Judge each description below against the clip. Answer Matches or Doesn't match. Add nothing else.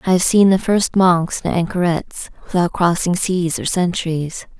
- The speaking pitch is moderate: Matches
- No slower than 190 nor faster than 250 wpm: Doesn't match